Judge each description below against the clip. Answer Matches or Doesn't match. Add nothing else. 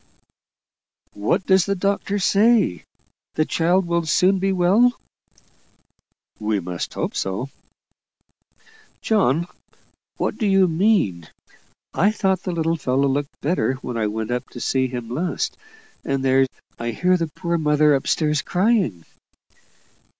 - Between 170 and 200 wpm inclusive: Doesn't match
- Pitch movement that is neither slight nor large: Doesn't match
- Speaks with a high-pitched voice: Doesn't match